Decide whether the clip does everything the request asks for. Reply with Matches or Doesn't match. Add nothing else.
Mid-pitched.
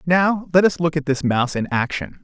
Matches